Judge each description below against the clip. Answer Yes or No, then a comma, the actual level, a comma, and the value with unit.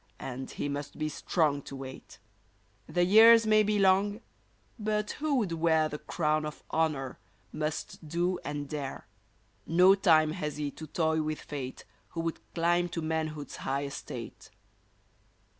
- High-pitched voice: No, medium, 160 Hz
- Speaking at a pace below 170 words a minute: Yes, average, 150 wpm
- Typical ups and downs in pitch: Yes, average, 3.6 semitones